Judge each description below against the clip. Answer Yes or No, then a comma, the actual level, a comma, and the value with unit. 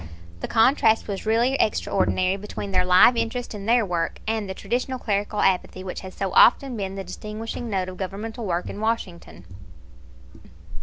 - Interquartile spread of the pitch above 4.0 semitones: No, average, 3.3 semitones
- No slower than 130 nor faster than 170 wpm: Yes, average, 165 wpm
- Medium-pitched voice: No, high, 205 Hz